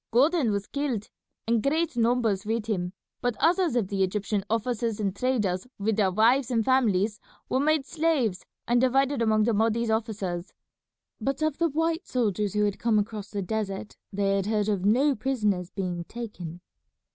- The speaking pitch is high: Yes, high, 220 Hz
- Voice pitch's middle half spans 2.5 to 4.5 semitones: Yes, average, 4.1 semitones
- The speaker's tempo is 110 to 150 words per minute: No, average, 170 wpm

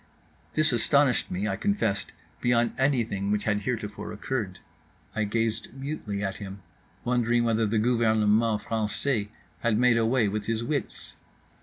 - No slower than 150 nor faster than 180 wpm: No, average, 140 wpm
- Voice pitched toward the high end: No, low, 115 Hz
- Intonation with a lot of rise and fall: No, average, 2.7 semitones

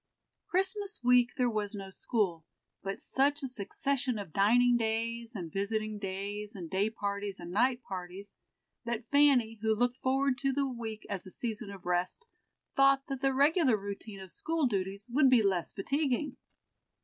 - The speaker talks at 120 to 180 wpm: Yes, average, 165 wpm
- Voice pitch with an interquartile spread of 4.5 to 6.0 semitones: Yes, average, 4.8 semitones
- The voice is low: No, high, 225 Hz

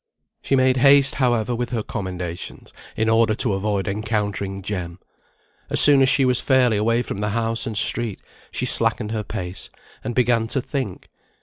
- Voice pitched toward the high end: No, low, 115 Hz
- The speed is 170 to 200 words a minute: Yes, average, 175 wpm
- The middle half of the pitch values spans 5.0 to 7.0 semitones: No, average, 3.4 semitones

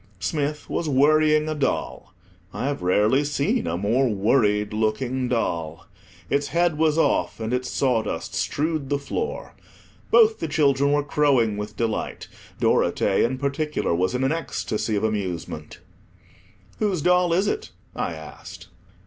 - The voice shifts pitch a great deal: Yes, wide, 6.1 semitones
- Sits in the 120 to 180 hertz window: Yes, low, 135 Hz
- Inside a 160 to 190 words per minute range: No, average, 145 wpm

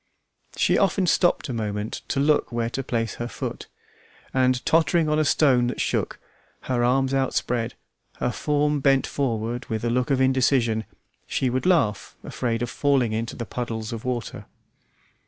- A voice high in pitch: No, low, 125 Hz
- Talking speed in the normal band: Yes, average, 165 wpm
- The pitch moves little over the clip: No, average, 3.0 semitones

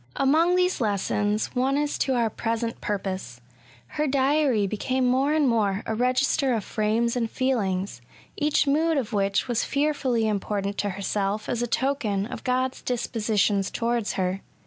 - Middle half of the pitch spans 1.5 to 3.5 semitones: No, average, 4.5 semitones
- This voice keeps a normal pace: Yes, average, 155 wpm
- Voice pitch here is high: Yes, high, 235 Hz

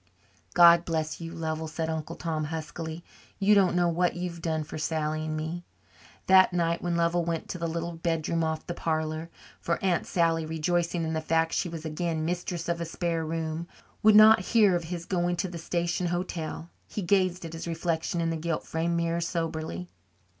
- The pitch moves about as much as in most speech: No, narrow, 1.4 semitones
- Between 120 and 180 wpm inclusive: No, average, 195 wpm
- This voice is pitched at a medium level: Yes, medium, 165 Hz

